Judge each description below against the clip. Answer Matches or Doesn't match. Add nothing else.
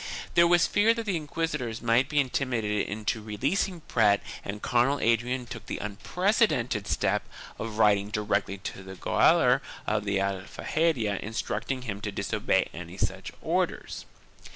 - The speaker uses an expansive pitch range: Matches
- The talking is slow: Doesn't match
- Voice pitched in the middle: Doesn't match